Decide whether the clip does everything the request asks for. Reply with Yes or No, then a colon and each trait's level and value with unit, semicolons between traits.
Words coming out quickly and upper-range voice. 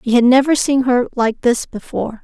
Yes: fast, 215 wpm; very high, 250 Hz